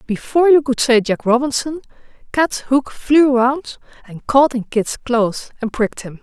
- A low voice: No, very high, 255 Hz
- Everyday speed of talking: Yes, average, 175 wpm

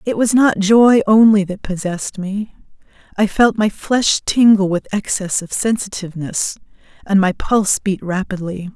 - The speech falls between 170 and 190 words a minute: No, average, 150 wpm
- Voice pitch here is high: Yes, high, 200 Hz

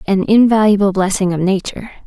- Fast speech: No, average, 145 wpm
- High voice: Yes, high, 200 Hz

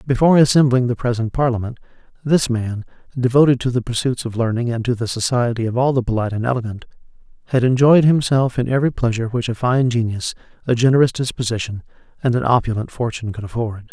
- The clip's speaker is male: Yes, male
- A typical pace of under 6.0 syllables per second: No, 6.6 syllables/s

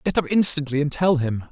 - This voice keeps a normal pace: No, fast, 240 wpm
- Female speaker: No, male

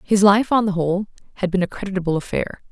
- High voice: Yes, high, 195 Hz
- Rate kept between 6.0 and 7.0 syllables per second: Yes, 6.8 syllables/s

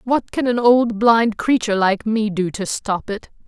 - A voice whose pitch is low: No, high, 220 Hz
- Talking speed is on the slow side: No, fast, 205 wpm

